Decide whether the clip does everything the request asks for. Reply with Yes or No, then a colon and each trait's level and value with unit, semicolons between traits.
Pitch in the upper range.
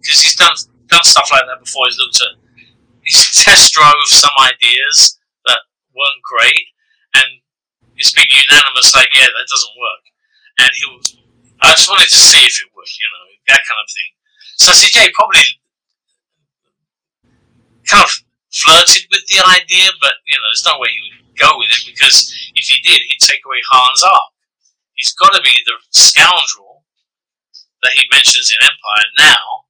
Yes: very high, 380 Hz